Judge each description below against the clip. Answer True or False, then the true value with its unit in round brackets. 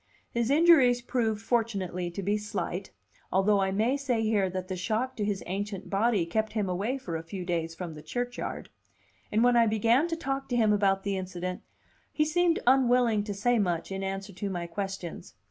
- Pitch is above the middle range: True (210 Hz)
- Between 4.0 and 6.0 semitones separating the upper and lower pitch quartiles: True (4.3 semitones)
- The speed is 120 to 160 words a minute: False (195 wpm)